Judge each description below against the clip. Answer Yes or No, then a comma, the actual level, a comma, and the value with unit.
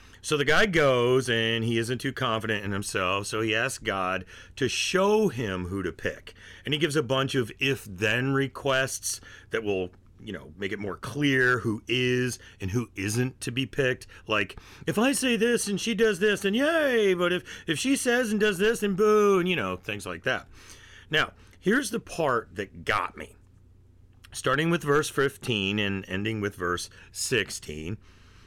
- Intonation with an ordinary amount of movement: No, wide, 7.8 semitones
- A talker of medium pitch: No, low, 120 Hz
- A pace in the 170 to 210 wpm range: Yes, average, 190 wpm